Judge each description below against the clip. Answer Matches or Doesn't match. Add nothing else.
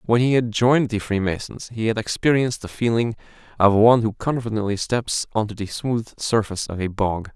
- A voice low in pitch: Matches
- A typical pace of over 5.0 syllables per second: Matches